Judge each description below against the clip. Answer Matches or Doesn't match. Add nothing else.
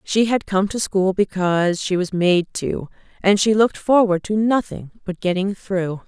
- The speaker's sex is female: Matches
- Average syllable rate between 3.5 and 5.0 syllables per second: Matches